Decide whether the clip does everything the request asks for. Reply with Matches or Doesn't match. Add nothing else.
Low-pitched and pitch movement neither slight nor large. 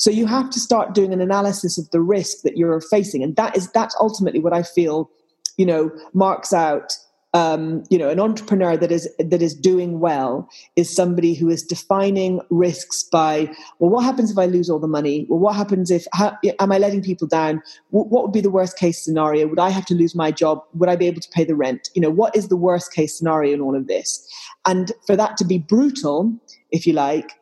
Doesn't match